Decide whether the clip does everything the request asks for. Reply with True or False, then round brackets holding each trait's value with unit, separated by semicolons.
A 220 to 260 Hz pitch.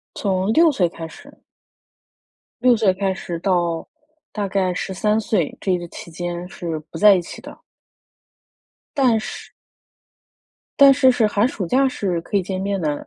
False (190 Hz)